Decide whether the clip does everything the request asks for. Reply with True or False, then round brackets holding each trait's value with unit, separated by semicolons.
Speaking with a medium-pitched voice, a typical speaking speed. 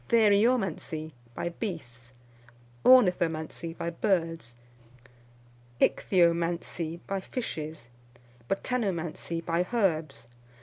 False (170 Hz; 70 wpm)